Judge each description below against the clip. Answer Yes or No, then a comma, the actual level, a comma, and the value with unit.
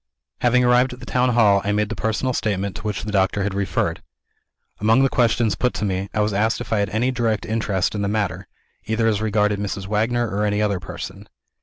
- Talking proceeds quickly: Yes, fast, 225 wpm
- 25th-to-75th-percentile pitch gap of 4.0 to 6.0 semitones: No, narrow, 2.4 semitones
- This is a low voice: Yes, low, 105 Hz